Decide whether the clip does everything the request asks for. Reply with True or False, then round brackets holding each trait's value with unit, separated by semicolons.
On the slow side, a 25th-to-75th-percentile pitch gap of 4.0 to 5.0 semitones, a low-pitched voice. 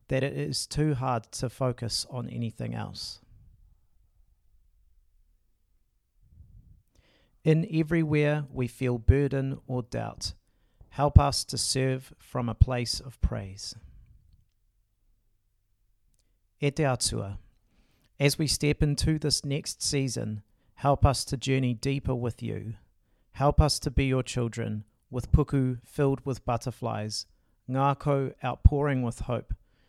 True (110 wpm; 4.5 semitones; 120 Hz)